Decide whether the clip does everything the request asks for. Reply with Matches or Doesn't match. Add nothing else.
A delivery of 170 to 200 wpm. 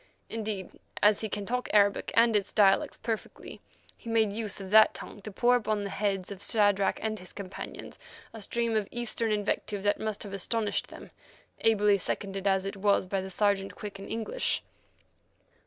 Matches